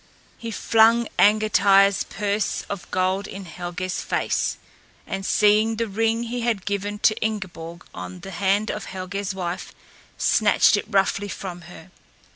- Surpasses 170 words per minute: No, average, 140 wpm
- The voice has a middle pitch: No, high, 200 Hz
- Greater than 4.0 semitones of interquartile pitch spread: No, narrow, 2.4 semitones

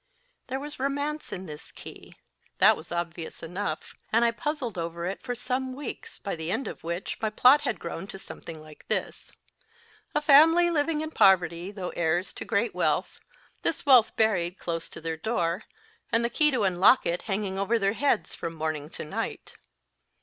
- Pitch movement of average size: No, wide, 7.4 semitones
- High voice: Yes, high, 200 Hz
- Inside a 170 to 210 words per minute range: Yes, average, 185 wpm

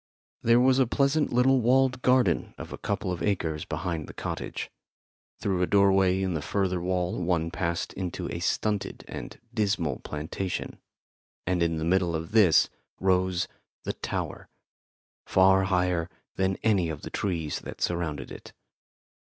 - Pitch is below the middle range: Yes, very low, 95 Hz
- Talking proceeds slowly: No, average, 155 wpm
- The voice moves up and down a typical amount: Yes, average, 3.4 semitones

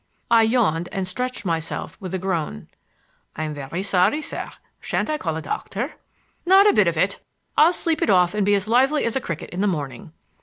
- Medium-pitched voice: No, high, 195 Hz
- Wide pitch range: Yes, wide, 6.6 semitones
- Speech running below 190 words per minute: No, fast, 205 wpm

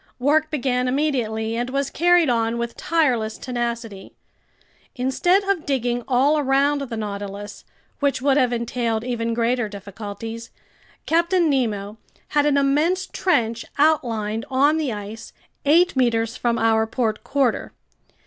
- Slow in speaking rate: Yes, slow, 130 wpm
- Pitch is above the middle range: Yes, high, 245 Hz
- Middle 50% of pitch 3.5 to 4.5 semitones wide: Yes, average, 4.2 semitones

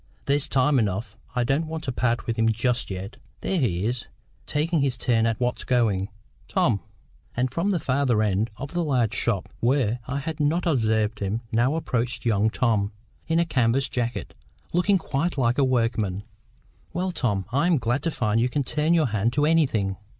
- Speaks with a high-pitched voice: No, low, 125 Hz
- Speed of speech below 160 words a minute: No, average, 190 wpm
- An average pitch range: Yes, average, 4.7 semitones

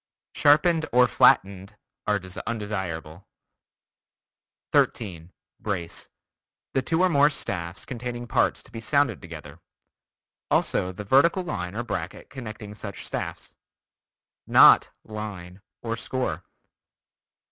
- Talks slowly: Yes, slow, 105 wpm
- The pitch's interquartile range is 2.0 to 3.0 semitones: No, wide, 5.6 semitones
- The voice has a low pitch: Yes, low, 105 Hz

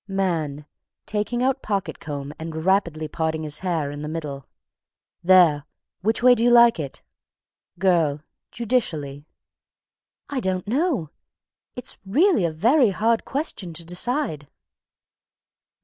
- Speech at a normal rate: No, slow, 125 wpm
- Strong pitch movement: Yes, wide, 6.9 semitones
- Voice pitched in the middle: Yes, medium, 180 Hz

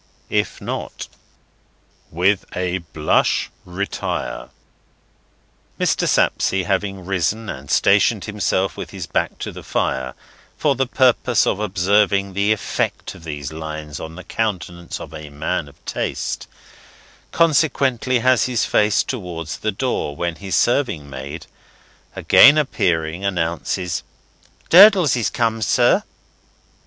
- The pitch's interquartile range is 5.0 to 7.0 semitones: Yes, wide, 5.5 semitones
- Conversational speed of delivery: No, slow, 125 wpm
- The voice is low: Yes, very low, 95 Hz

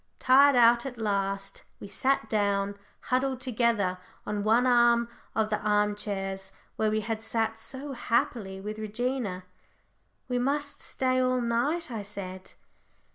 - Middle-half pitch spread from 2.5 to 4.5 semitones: Yes, average, 3.7 semitones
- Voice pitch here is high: Yes, high, 225 Hz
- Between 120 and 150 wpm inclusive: Yes, slow, 135 wpm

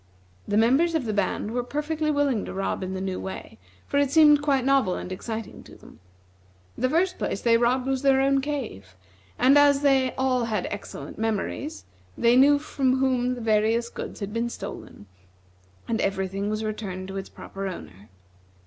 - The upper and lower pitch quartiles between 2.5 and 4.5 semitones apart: No, average, 5.0 semitones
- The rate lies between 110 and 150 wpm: No, average, 185 wpm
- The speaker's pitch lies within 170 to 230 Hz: No, high, 245 Hz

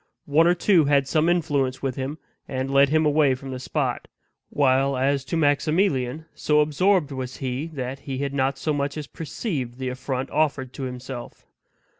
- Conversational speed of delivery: Yes, average, 180 wpm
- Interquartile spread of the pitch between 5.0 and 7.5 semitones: No, average, 2.7 semitones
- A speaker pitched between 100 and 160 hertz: Yes, medium, 140 Hz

